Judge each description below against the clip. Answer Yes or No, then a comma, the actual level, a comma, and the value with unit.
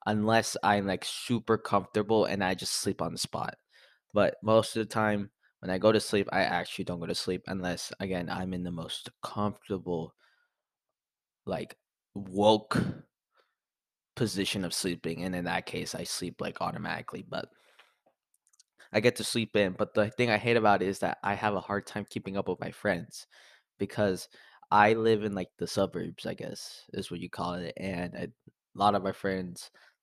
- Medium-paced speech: Yes, average, 190 wpm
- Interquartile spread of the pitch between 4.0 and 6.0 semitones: No, narrow, 2.6 semitones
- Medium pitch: No, low, 100 Hz